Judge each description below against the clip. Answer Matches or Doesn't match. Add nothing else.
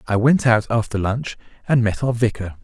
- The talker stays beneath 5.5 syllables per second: Matches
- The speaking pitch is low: Matches